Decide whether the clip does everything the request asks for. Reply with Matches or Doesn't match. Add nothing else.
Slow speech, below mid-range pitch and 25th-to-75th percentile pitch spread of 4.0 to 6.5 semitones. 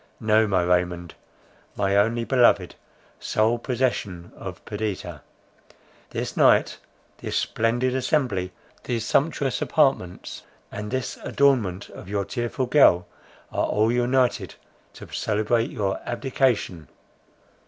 Matches